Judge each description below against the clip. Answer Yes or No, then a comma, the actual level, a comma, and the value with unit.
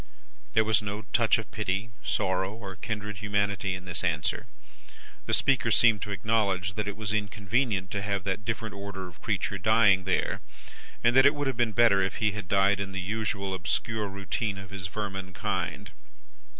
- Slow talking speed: No, average, 185 wpm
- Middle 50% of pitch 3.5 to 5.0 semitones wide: No, narrow, 2.4 semitones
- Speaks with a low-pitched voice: Yes, low, 100 Hz